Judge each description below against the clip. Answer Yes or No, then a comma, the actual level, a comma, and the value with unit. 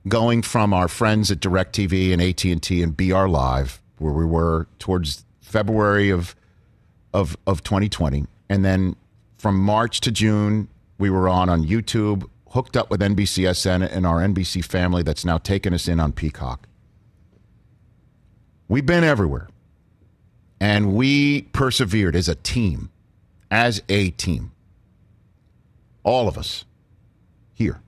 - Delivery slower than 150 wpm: Yes, slow, 135 wpm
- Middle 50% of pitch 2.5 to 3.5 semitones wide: Yes, average, 3.2 semitones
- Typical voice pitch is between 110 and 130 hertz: No, very low, 95 Hz